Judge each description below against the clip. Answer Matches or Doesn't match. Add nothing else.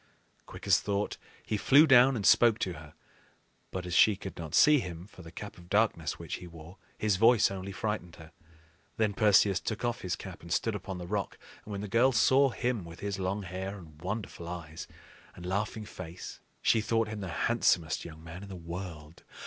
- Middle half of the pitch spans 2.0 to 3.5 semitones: Doesn't match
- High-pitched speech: Doesn't match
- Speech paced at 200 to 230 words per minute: Matches